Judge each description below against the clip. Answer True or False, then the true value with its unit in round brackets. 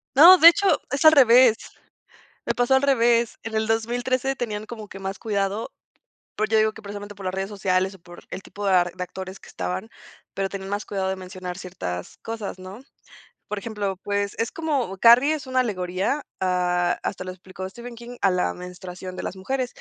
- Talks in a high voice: True (205 Hz)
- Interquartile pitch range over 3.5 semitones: True (4.1 semitones)